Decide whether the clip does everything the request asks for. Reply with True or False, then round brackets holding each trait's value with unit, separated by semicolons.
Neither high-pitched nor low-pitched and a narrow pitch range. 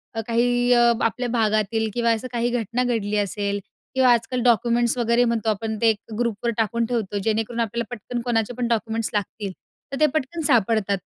False (230 Hz; 1.9 semitones)